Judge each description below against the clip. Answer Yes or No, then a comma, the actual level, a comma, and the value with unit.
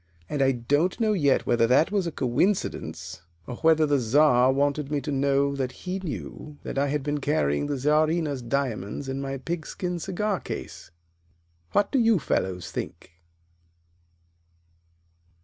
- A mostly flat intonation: No, average, 3.6 semitones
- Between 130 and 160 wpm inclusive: Yes, average, 150 wpm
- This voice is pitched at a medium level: Yes, medium, 145 Hz